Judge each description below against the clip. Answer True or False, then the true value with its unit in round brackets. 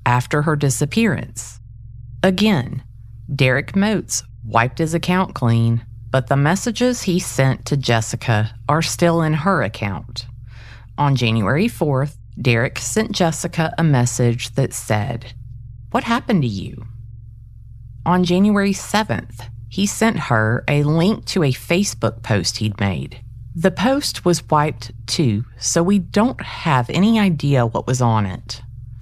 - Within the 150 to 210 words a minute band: False (135 wpm)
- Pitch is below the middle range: True (125 Hz)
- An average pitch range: False (6.8 semitones)